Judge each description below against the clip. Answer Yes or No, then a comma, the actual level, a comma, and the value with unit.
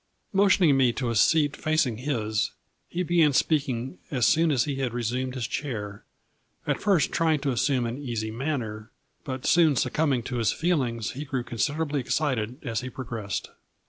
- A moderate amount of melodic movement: Yes, average, 4.4 semitones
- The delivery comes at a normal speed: Yes, average, 175 wpm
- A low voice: Yes, low, 130 Hz